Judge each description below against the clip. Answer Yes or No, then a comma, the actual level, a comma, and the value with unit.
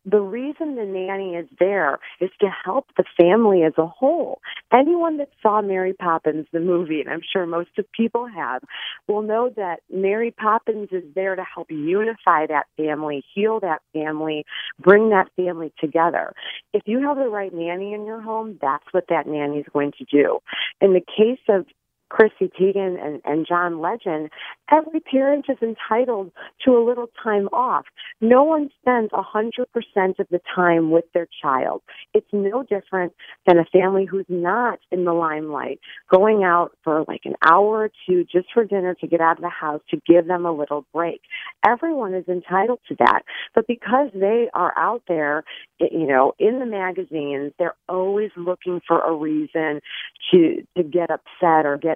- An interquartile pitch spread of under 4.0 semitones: No, average, 4.9 semitones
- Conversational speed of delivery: Yes, average, 180 wpm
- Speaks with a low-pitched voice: No, medium, 185 Hz